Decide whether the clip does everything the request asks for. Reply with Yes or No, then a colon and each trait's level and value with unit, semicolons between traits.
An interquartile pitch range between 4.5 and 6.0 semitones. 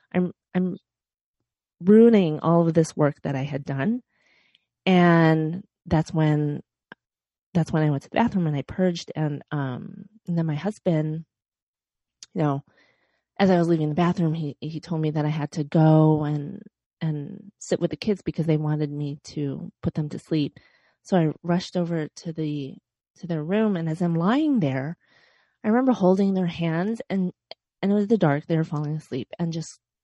No: average, 3.3 semitones